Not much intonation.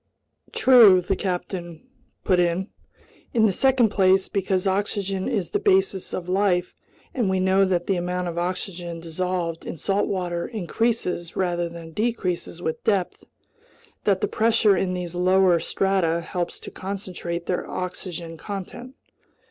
Yes: narrow, 2.1 semitones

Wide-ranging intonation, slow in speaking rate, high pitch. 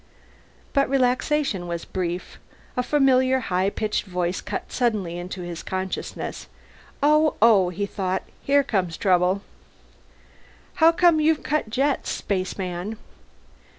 Yes: wide, 6.9 semitones; slow, 120 wpm; high, 205 Hz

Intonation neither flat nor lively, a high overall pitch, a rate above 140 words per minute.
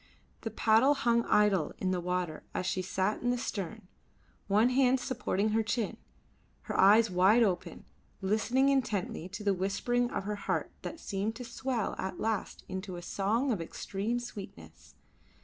Yes: average, 4.0 semitones; high, 210 Hz; average, 165 wpm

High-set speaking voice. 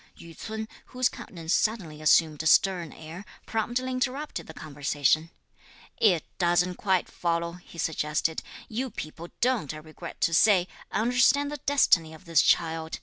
No: medium, 175 Hz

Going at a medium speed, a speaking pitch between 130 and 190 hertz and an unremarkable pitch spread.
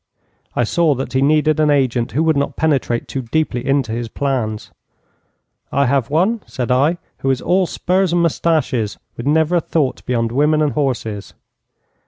Yes: average, 175 wpm; medium, 140 Hz; average, 4.3 semitones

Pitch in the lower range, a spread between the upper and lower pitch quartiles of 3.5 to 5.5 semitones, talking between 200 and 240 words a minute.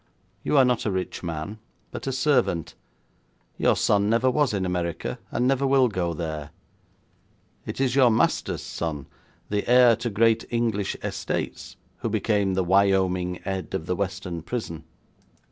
No: low, 100 Hz; average, 5.1 semitones; average, 155 wpm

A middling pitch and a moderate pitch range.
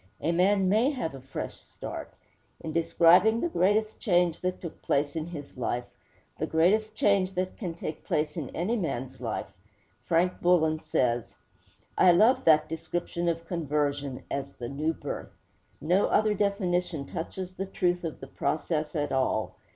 Yes: medium, 170 Hz; average, 3.7 semitones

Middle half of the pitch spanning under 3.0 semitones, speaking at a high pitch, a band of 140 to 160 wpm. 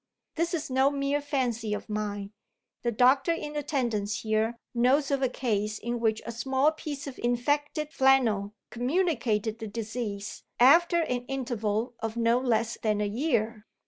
No: average, 4.2 semitones; high, 240 Hz; average, 155 wpm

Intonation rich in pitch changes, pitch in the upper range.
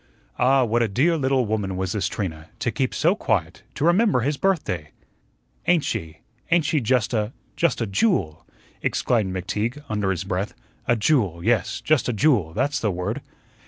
No: wide, 6.9 semitones; low, 115 Hz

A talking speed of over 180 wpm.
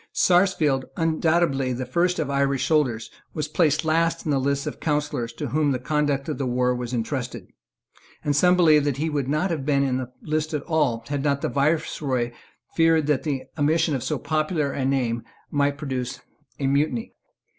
Yes: average, 190 wpm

